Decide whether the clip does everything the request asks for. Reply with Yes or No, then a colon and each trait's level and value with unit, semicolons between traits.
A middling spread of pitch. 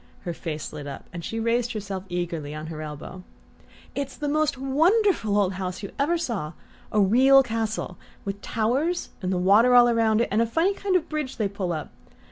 No: wide, 6.8 semitones